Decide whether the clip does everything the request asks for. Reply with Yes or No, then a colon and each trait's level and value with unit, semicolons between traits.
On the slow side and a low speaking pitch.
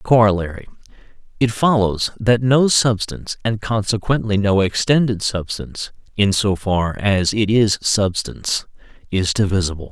Yes: slow, 115 wpm; low, 105 Hz